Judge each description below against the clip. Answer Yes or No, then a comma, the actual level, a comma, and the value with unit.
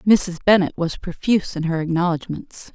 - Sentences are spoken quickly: No, average, 155 wpm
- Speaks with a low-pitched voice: No, medium, 180 Hz